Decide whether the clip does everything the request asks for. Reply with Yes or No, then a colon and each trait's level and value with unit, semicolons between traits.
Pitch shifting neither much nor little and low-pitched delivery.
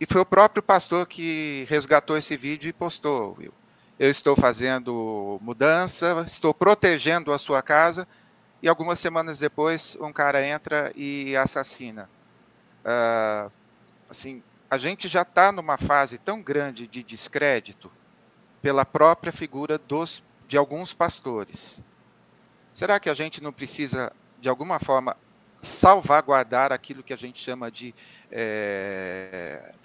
No: average, 4.3 semitones; medium, 145 Hz